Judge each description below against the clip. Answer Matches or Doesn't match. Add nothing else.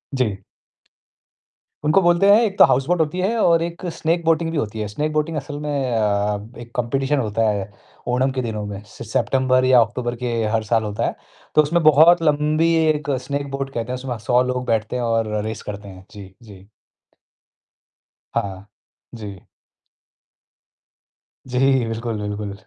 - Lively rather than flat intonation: Matches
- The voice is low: Matches